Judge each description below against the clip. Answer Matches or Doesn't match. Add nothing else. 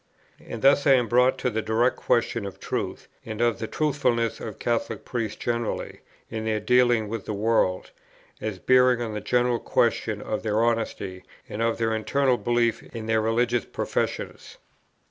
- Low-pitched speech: Matches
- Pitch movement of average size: Doesn't match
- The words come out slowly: Doesn't match